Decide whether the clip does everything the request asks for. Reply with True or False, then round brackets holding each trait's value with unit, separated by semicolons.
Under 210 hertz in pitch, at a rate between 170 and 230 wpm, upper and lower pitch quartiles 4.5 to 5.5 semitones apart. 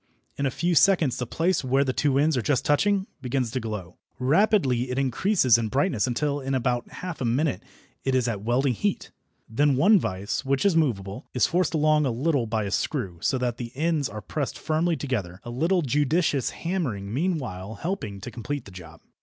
True (135 Hz; 200 wpm; 5.2 semitones)